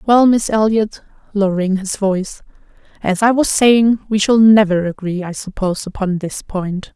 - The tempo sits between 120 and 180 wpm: Yes, average, 165 wpm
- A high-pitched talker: Yes, high, 205 Hz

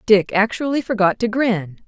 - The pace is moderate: Yes, average, 160 wpm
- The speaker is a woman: Yes, female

